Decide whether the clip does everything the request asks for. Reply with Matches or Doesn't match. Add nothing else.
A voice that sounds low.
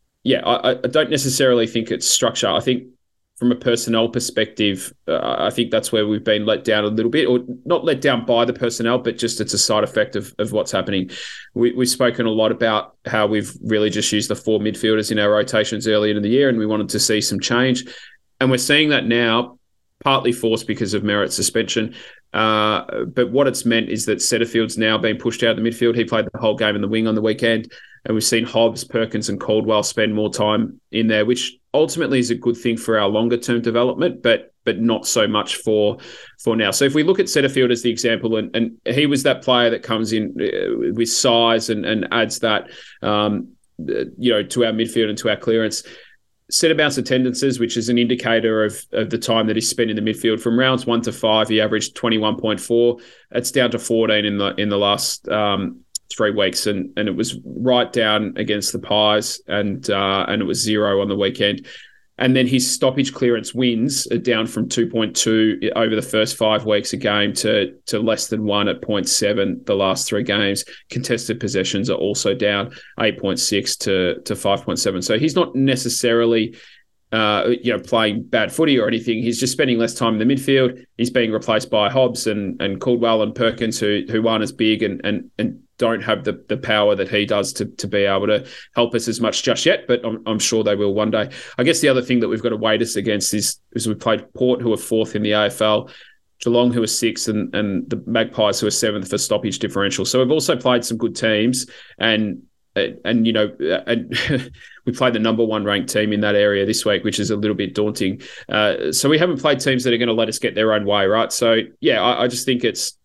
Matches